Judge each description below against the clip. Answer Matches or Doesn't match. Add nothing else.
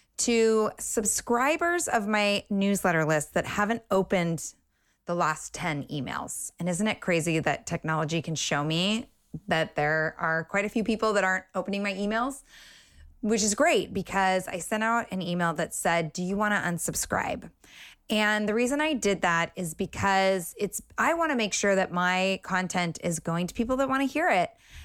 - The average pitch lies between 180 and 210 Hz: Matches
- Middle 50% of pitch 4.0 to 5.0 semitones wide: Matches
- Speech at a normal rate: Matches